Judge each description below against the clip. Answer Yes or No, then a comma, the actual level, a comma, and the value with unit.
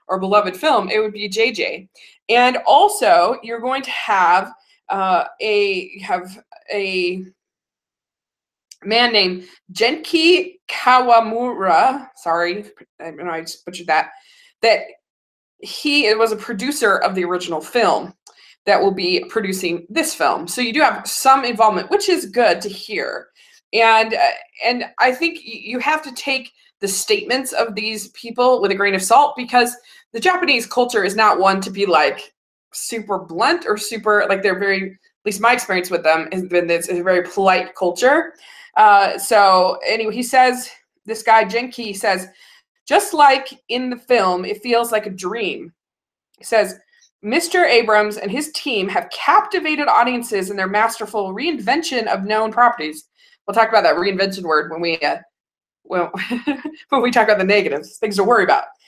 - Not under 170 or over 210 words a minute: No, average, 160 wpm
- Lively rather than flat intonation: Yes, wide, 6.3 semitones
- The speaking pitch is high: Yes, high, 225 Hz